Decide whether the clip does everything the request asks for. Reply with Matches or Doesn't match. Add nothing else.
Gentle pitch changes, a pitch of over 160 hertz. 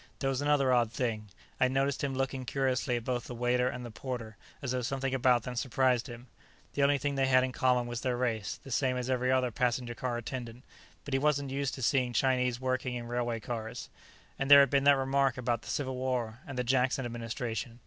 Doesn't match